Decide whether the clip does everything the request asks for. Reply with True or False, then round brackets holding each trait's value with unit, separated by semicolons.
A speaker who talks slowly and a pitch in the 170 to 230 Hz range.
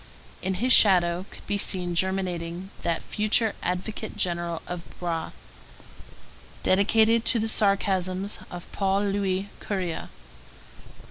True (115 wpm; 190 Hz)